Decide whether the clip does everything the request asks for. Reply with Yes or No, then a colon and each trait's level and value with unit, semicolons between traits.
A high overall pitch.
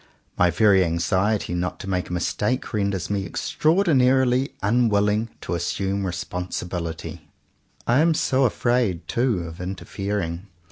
No: low, 100 Hz